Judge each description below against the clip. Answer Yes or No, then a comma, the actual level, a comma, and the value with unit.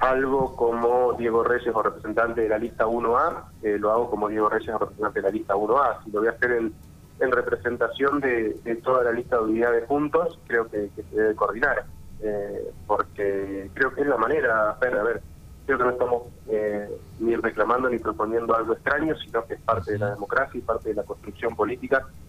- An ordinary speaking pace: No, fast, 210 wpm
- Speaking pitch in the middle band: No, low, 115 Hz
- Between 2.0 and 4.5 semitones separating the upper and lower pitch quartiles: Yes, average, 2.8 semitones